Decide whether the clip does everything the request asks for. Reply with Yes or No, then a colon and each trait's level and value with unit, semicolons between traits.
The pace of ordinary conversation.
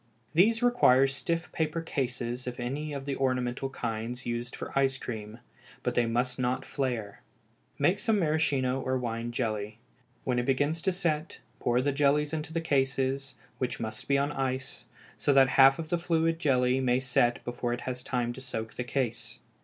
Yes: average, 180 wpm